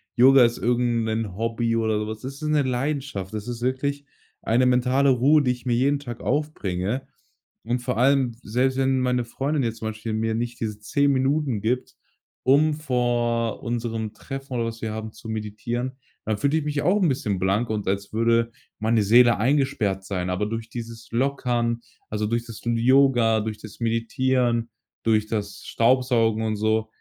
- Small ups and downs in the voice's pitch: No, average, 3.0 semitones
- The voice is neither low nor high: No, low, 120 Hz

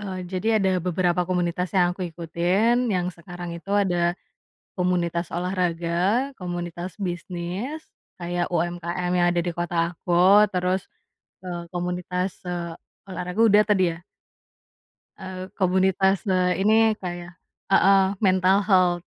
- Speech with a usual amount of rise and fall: No, narrow, 1.6 semitones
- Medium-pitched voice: Yes, medium, 180 Hz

